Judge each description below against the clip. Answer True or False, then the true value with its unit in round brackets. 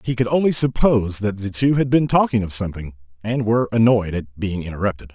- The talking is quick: True (210 wpm)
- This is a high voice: False (110 Hz)